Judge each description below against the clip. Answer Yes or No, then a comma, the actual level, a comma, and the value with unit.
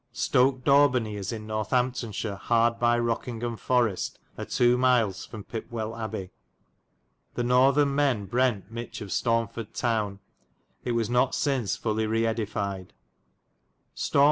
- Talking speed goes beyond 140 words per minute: No, slow, 135 wpm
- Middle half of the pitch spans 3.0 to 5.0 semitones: No, narrow, 2.5 semitones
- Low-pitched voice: Yes, low, 115 Hz